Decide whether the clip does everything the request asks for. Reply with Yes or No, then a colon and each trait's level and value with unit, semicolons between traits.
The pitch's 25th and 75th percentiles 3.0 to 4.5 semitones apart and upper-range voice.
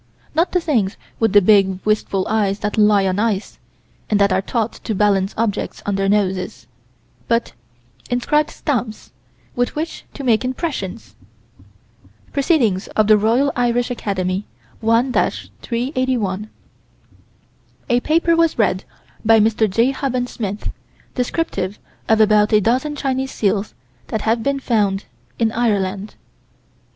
Yes: average, 3.7 semitones; high, 220 Hz